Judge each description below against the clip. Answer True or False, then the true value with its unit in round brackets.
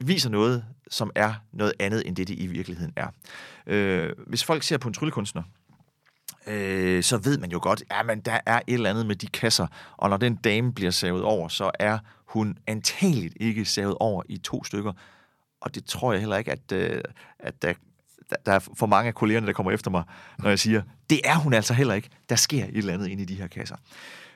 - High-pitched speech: False (110 Hz)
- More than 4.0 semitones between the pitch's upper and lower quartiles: False (3.3 semitones)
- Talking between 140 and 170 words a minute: False (225 wpm)